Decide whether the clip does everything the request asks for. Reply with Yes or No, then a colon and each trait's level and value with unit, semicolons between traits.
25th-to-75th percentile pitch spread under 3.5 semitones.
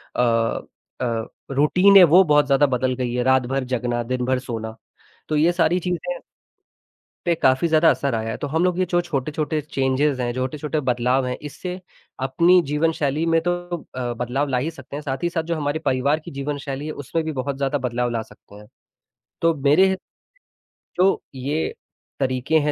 No: average, 3.9 semitones